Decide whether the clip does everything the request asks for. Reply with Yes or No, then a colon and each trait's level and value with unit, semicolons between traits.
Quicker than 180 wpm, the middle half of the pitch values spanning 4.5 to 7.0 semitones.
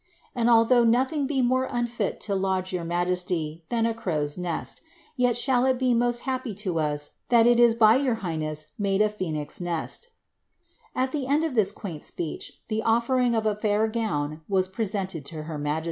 Yes: average, 190 wpm; wide, 5.6 semitones